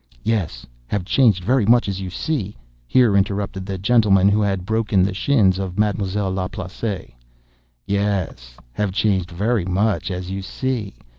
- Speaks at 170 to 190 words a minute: No, average, 140 wpm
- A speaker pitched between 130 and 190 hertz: No, low, 100 Hz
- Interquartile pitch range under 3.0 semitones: Yes, narrow, 2.4 semitones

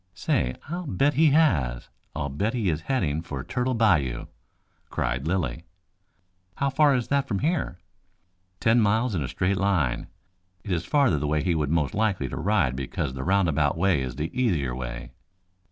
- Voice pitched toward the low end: Yes, very low, 90 Hz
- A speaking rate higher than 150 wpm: Yes, average, 180 wpm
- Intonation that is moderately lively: No, wide, 8.6 semitones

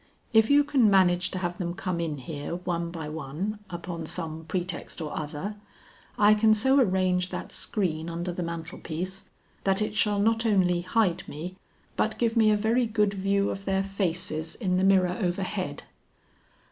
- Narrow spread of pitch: No, average, 3.5 semitones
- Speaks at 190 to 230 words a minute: No, average, 175 wpm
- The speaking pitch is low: No, medium, 185 Hz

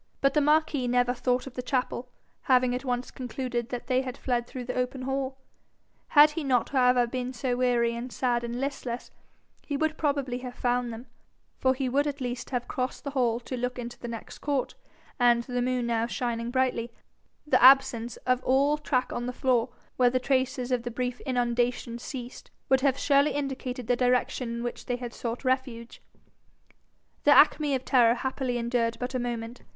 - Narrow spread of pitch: Yes, narrow, 1.6 semitones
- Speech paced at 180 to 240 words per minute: Yes, average, 190 wpm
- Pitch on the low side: No, very high, 250 Hz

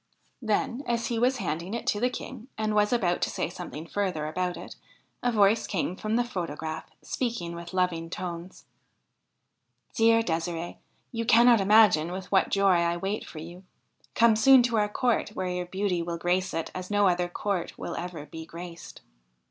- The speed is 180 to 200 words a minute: Yes, average, 185 wpm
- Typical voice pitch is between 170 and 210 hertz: Yes, medium, 185 Hz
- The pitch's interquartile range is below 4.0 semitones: No, average, 4.4 semitones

